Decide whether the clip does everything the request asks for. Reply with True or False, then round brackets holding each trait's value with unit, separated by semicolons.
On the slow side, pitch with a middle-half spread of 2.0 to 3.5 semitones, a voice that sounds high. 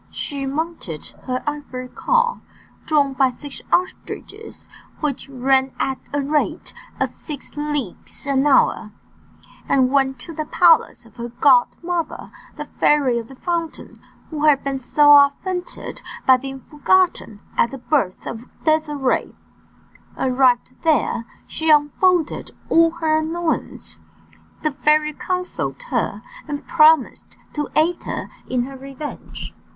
True (130 wpm; 3.2 semitones; 290 Hz)